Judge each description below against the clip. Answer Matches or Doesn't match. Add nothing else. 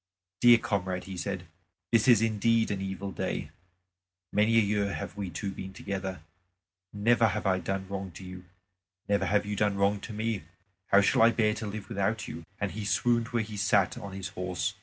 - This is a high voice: Doesn't match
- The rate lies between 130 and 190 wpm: Doesn't match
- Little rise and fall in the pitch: Matches